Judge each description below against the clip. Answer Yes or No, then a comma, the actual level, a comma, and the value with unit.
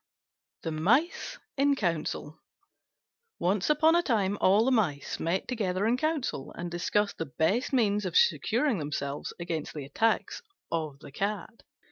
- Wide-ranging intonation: Yes, wide, 6.6 semitones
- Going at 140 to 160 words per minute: Yes, average, 145 wpm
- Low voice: No, high, 195 Hz